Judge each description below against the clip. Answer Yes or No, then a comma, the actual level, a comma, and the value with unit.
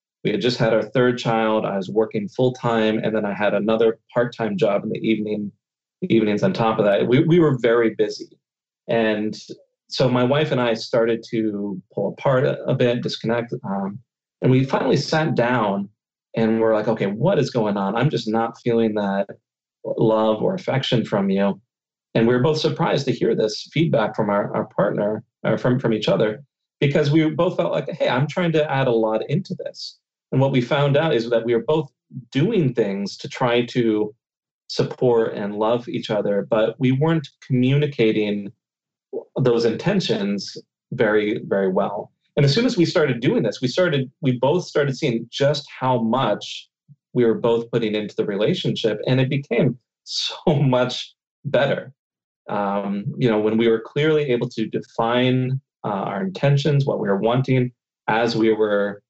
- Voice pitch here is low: Yes, low, 115 Hz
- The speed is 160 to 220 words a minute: Yes, average, 185 wpm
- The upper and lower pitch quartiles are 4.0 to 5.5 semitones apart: Yes, average, 4.3 semitones